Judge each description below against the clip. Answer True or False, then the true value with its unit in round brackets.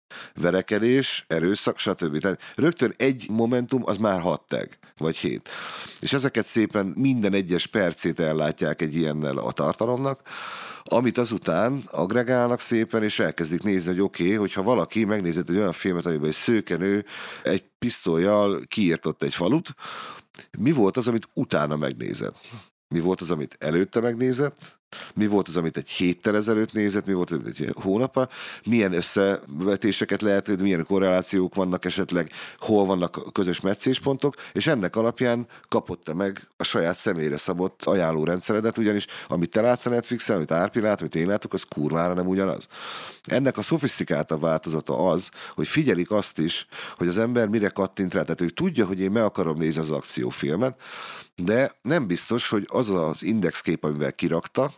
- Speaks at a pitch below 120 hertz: True (95 Hz)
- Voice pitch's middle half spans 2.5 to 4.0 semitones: False (4.7 semitones)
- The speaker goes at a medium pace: False (160 wpm)